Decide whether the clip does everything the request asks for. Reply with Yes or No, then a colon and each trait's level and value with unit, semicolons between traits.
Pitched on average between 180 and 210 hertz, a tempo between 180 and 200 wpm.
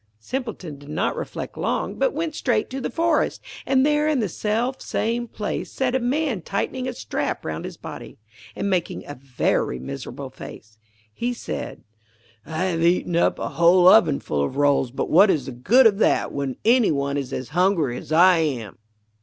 Yes: medium, 185 Hz; average, 185 wpm